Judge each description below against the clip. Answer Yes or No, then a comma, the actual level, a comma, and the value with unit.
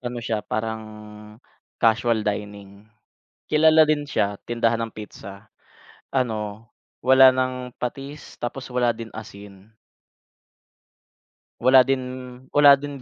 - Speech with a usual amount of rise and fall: Yes, average, 3.6 semitones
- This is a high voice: No, low, 120 Hz